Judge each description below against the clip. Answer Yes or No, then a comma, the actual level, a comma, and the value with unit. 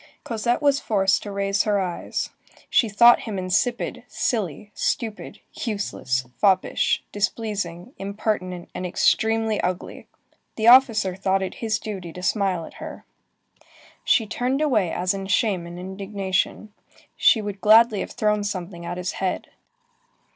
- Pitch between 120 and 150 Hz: No, high, 200 Hz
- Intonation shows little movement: No, average, 3.2 semitones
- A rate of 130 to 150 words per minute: Yes, average, 140 wpm